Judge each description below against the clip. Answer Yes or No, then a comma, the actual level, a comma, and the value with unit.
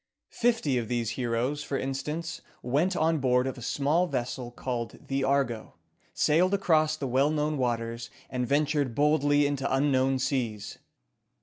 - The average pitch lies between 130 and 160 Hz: Yes, low, 135 Hz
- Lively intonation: No, average, 3.3 semitones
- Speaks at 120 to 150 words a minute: Yes, average, 145 wpm